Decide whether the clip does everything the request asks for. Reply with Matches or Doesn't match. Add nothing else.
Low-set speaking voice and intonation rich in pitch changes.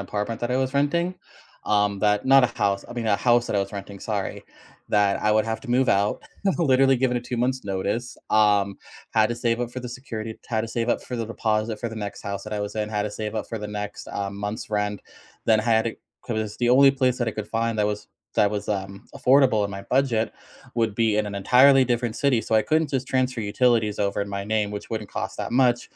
Doesn't match